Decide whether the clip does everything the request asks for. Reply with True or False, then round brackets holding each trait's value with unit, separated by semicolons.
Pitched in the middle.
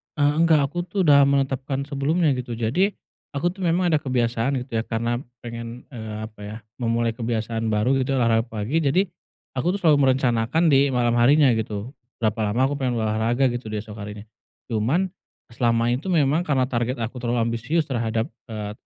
False (125 Hz)